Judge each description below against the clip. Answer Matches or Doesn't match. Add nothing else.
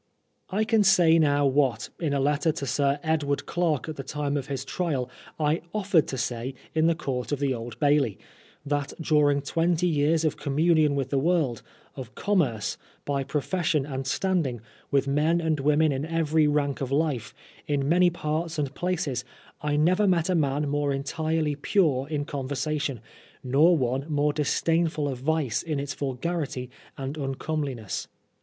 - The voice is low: Doesn't match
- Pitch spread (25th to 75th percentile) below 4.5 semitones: Matches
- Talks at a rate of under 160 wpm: Doesn't match